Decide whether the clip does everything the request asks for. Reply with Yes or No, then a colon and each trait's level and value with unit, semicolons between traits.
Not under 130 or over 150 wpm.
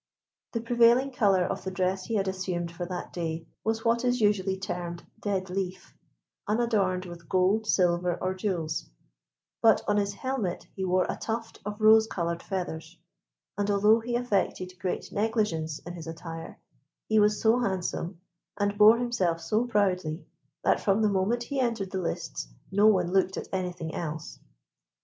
No: average, 165 wpm